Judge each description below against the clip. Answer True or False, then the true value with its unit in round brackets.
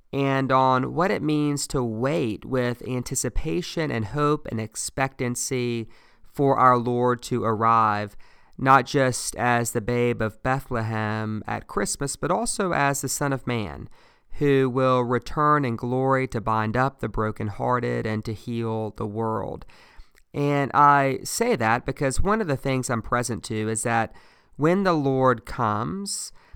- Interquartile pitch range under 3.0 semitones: False (3.5 semitones)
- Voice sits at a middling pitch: False (125 Hz)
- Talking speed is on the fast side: False (150 wpm)